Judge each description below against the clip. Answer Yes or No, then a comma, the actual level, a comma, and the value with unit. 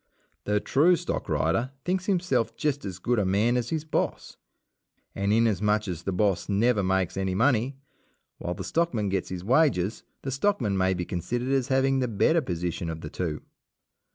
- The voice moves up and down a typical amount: No, wide, 6.1 semitones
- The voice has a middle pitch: No, low, 105 Hz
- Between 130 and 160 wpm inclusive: No, average, 175 wpm